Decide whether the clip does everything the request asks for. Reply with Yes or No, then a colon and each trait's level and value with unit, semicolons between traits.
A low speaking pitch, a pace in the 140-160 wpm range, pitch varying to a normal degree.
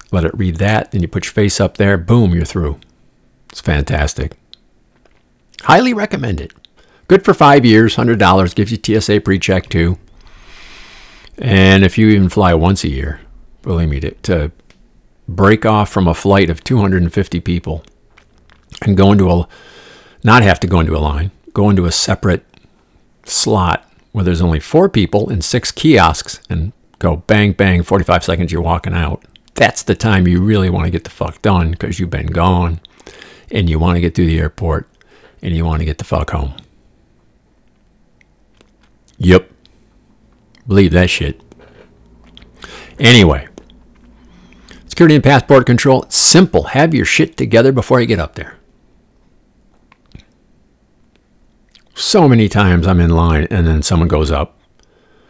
Yes: very low, 95 Hz; average, 155 wpm; average, 4.0 semitones